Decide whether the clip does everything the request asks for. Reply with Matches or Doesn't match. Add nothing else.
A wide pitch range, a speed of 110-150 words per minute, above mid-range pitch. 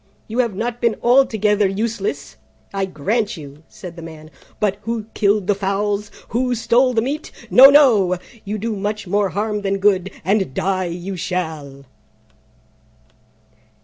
Doesn't match